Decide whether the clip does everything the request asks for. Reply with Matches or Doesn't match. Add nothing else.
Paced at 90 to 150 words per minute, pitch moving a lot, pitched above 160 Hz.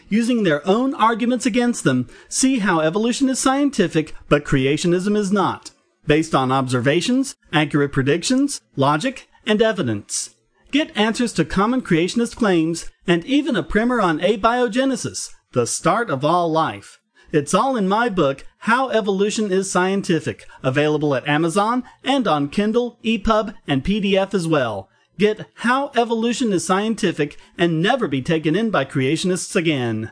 Matches